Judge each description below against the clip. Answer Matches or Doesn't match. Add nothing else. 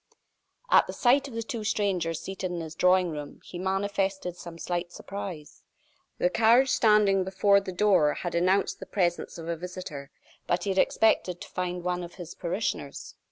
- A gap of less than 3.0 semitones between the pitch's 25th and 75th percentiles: Matches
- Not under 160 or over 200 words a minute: Matches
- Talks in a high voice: Doesn't match